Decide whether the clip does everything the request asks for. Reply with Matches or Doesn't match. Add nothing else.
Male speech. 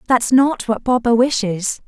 Doesn't match